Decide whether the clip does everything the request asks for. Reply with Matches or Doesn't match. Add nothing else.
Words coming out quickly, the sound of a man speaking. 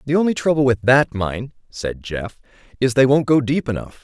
Matches